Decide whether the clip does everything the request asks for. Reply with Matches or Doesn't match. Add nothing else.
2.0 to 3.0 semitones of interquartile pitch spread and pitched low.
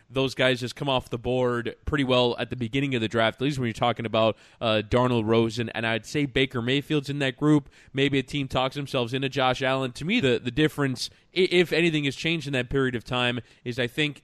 Matches